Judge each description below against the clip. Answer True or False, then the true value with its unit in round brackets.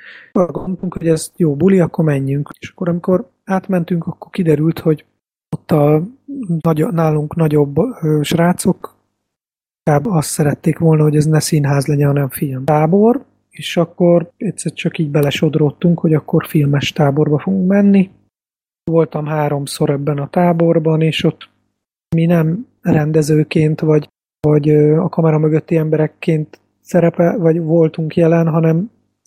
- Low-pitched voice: False (160 Hz)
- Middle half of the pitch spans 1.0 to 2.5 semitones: True (2.2 semitones)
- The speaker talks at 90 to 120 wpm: False (135 wpm)